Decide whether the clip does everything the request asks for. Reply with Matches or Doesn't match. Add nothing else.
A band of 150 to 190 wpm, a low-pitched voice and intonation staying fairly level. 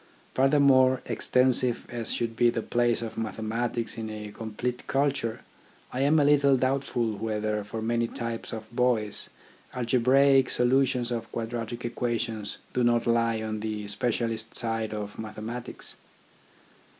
Doesn't match